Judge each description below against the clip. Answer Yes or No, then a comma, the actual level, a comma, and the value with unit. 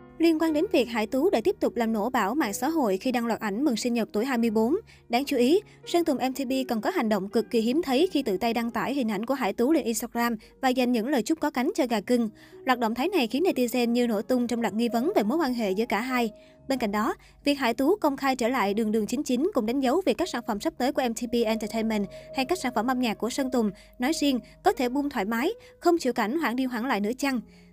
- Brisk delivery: Yes, fast, 280 wpm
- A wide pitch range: No, average, 4.1 semitones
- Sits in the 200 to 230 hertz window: No, high, 245 Hz